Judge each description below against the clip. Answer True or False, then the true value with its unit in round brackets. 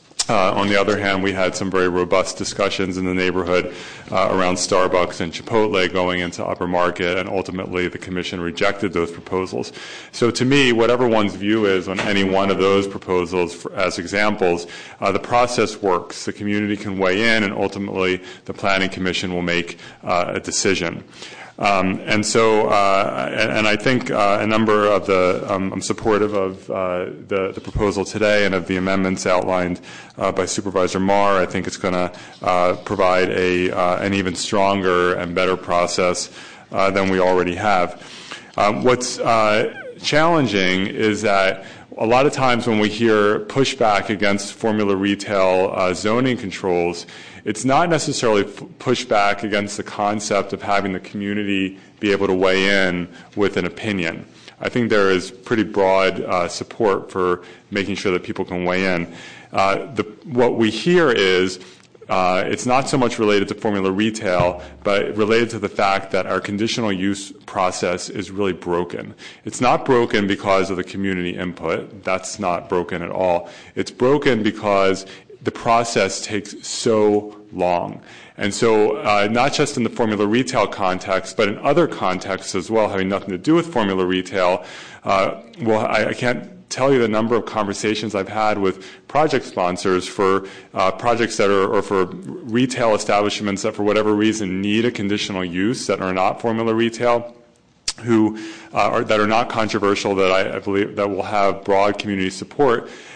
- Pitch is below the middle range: True (100 Hz)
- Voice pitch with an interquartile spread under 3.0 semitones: True (2.6 semitones)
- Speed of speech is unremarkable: True (175 wpm)